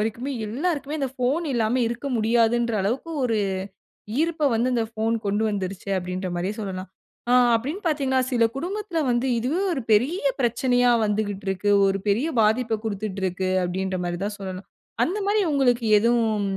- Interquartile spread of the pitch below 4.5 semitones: No, average, 4.8 semitones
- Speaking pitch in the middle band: No, high, 230 Hz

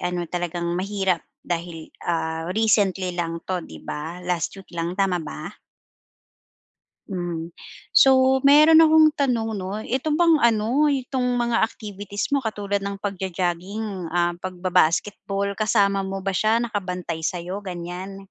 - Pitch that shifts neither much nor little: Yes, average, 4.0 semitones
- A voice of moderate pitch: No, high, 195 Hz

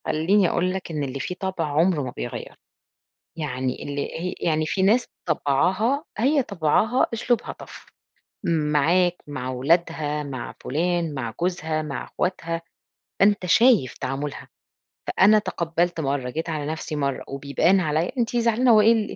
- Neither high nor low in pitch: Yes, medium, 165 Hz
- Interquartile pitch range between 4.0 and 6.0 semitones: Yes, average, 4.6 semitones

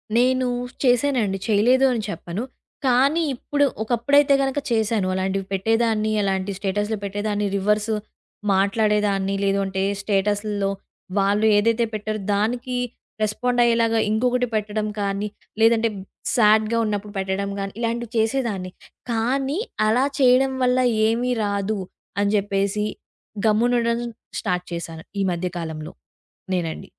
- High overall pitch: Yes, high, 215 Hz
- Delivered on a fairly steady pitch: No, average, 3.2 semitones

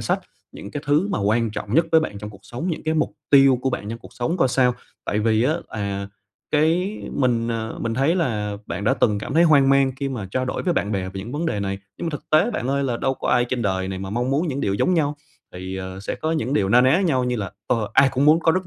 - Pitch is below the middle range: Yes, low, 125 Hz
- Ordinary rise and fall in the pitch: No, wide, 6.3 semitones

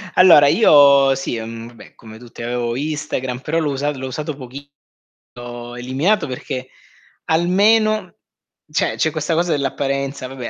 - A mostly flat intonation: No, average, 3.9 semitones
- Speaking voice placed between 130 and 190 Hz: Yes, medium, 140 Hz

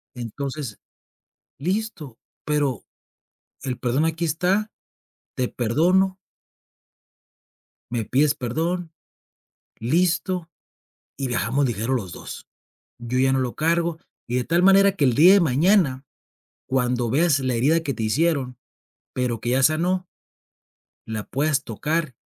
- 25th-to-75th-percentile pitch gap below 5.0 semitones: No, average, 5.3 semitones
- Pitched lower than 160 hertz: Yes, medium, 140 Hz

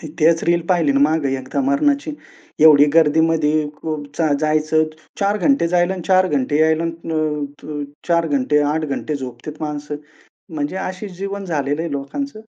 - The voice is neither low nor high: Yes, medium, 155 Hz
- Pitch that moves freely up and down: No, average, 3.0 semitones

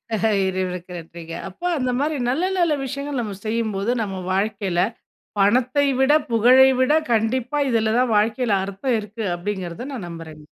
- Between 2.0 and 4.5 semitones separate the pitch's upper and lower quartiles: No, average, 5.0 semitones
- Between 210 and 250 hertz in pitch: Yes, high, 220 Hz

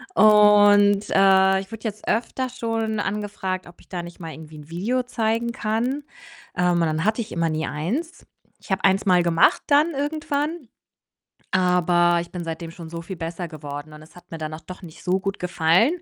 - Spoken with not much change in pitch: No, average, 4.7 semitones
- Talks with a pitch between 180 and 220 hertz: Yes, high, 190 Hz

